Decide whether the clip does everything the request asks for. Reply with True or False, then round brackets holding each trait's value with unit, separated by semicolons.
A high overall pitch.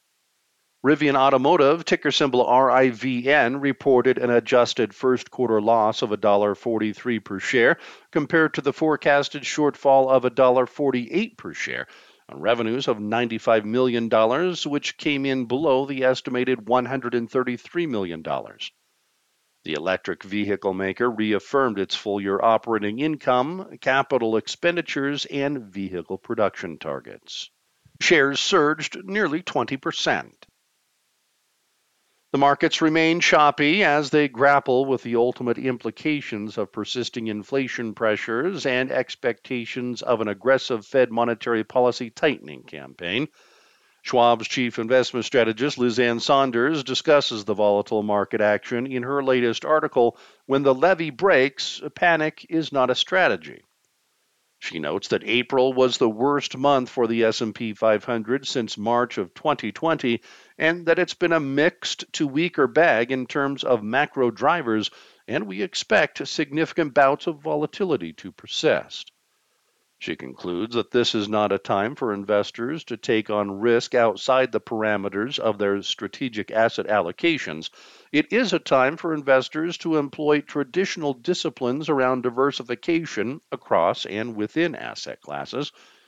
False (130 Hz)